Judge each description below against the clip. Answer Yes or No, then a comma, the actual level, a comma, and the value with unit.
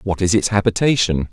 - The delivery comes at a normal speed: Yes, average, 180 wpm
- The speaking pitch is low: Yes, low, 100 Hz